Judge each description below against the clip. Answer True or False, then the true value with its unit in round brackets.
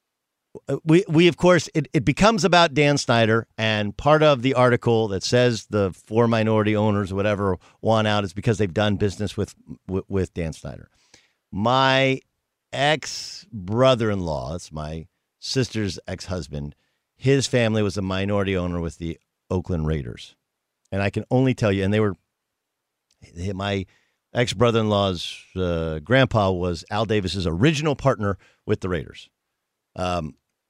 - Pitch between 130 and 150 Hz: False (105 Hz)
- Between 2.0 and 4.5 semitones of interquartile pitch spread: False (4.9 semitones)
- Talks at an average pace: True (145 wpm)